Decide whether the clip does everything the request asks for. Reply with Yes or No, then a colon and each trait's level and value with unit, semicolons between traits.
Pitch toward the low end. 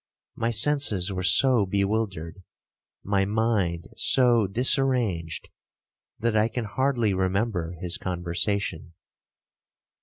Yes: low, 100 Hz